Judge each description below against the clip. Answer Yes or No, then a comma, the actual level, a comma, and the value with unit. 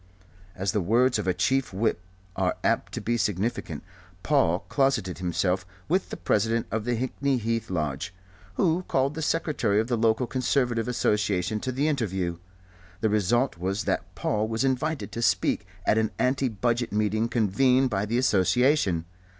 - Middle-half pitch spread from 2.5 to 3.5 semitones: No, average, 4.7 semitones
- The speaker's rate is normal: Yes, average, 165 wpm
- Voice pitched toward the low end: Yes, low, 115 Hz